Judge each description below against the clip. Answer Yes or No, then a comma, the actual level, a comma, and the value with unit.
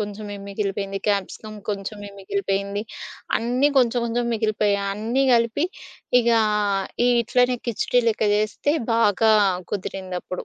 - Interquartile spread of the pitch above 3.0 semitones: No, average, 2.7 semitones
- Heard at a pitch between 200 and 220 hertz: Yes, high, 210 Hz